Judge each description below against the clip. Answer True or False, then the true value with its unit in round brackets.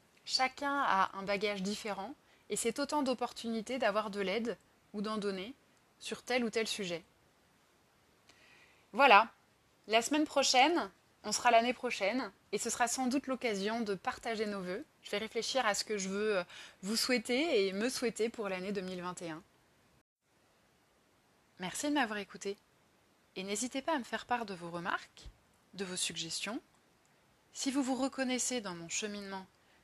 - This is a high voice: True (220 Hz)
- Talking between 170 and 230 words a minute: False (155 wpm)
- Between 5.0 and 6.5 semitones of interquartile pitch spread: False (4.2 semitones)